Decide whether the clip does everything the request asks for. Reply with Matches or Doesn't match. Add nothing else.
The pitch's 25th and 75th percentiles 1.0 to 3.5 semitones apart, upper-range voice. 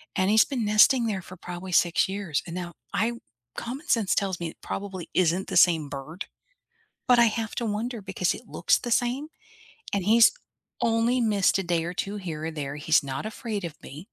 Doesn't match